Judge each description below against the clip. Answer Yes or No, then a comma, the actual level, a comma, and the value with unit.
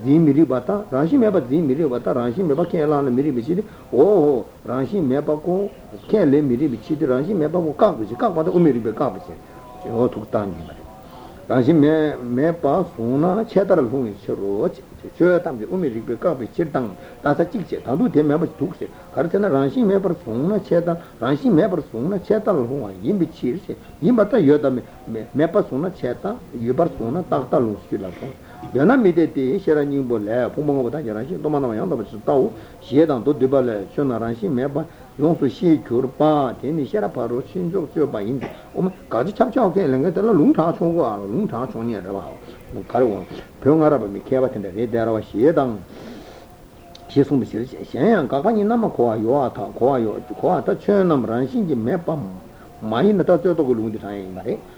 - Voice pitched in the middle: Yes, medium, 145 Hz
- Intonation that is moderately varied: No, wide, 5.7 semitones